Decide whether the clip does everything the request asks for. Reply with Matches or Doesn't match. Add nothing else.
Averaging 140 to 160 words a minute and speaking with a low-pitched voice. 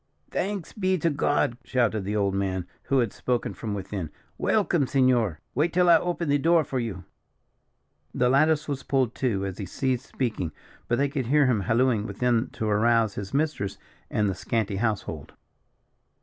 Doesn't match